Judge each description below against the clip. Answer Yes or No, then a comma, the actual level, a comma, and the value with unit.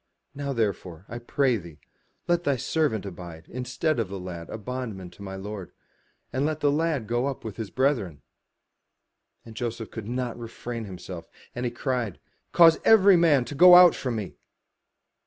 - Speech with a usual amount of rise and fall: No, wide, 6.1 semitones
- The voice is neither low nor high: No, low, 120 Hz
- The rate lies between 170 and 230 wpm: Yes, average, 175 wpm